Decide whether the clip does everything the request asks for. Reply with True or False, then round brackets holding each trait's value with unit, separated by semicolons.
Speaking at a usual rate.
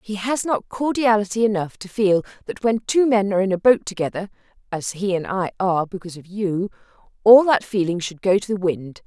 False (210 wpm)